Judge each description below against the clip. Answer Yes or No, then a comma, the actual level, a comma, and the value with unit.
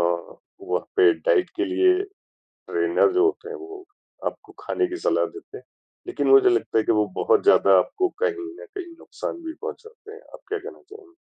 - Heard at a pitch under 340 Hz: No, very high, 380 Hz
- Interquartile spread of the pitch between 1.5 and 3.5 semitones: Yes, average, 3.0 semitones